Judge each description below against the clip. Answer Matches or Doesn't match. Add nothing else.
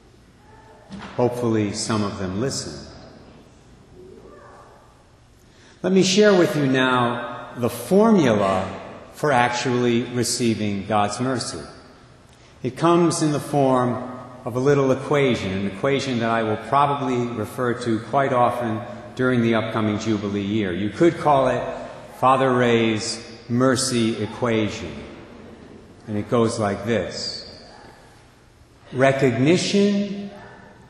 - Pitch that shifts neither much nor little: Matches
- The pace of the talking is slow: Matches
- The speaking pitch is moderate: Doesn't match